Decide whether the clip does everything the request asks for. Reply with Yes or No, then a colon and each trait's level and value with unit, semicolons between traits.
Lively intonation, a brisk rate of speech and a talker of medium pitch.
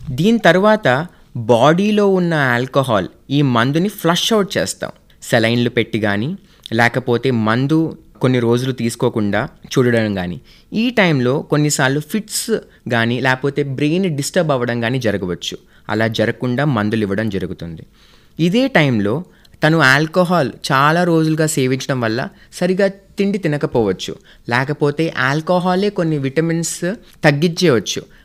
No: wide, 6.5 semitones; average, 110 wpm; medium, 145 Hz